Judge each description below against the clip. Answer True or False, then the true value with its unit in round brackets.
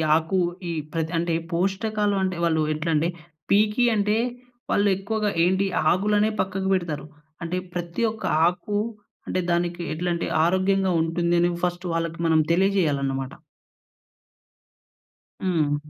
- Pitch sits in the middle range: True (175 Hz)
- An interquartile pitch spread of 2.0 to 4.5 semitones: True (2.7 semitones)